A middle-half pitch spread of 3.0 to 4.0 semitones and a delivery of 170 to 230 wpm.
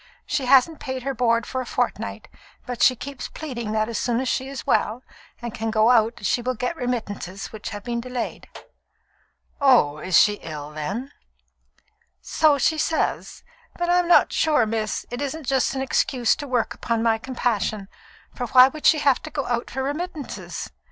Yes: average, 3.5 semitones; average, 185 wpm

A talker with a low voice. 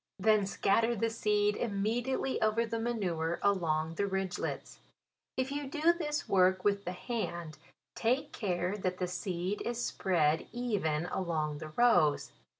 No: high, 200 Hz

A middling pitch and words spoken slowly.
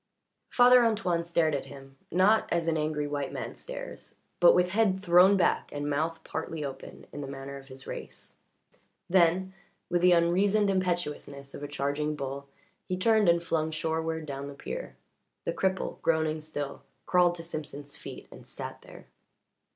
No: medium, 165 Hz; average, 165 wpm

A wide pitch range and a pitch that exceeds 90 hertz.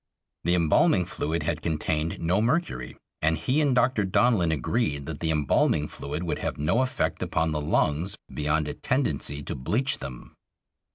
No: wide, 6.5 semitones; very low, 80 Hz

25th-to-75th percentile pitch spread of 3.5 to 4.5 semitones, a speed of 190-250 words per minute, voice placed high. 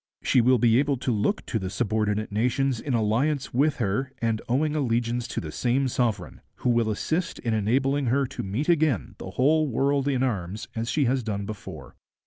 No: average, 3.9 semitones; average, 195 wpm; low, 120 Hz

